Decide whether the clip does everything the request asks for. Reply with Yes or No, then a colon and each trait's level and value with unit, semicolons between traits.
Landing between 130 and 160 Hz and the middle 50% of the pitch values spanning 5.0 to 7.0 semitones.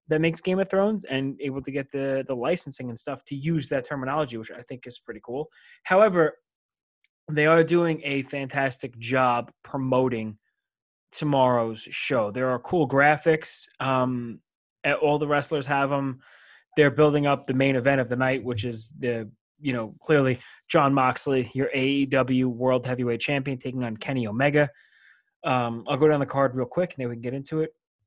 No: low, 135 Hz; average, 2.7 semitones